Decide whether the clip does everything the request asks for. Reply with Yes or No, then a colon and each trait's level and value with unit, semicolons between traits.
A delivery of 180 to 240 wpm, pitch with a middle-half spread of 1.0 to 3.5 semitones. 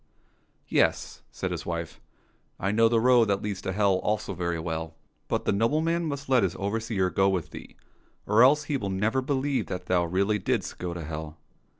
No: fast, 205 wpm; average, 5.2 semitones